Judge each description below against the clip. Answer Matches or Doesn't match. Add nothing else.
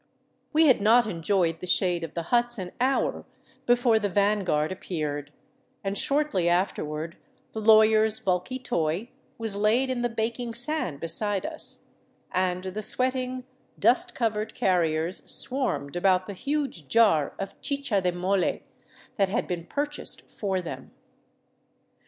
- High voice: Matches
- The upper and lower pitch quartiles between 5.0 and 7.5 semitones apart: Matches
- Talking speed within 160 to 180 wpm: Doesn't match